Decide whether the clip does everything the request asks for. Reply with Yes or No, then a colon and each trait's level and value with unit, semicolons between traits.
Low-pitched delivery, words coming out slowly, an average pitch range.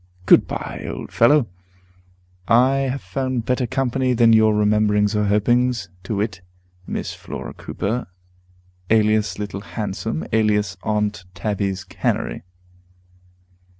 Yes: low, 110 Hz; slow, 115 wpm; average, 3.0 semitones